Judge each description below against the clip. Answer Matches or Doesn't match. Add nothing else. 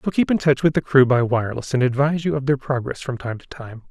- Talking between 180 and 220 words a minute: Doesn't match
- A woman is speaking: Doesn't match